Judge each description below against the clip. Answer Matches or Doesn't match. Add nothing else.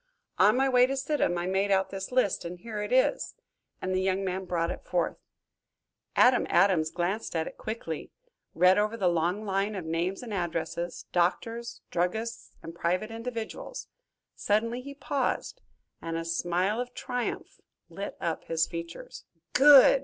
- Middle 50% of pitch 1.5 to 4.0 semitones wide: Doesn't match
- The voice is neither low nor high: Doesn't match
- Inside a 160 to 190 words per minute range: Matches